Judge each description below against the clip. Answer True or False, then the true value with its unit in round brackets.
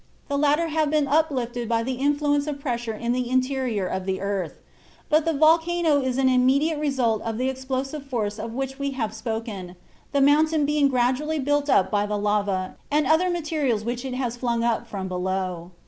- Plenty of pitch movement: False (4.6 semitones)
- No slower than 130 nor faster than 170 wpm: False (195 wpm)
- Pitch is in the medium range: False (260 Hz)